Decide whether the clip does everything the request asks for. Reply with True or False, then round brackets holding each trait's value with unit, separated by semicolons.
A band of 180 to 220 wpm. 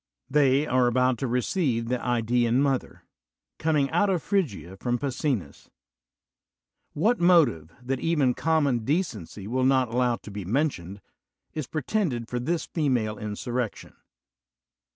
False (145 wpm)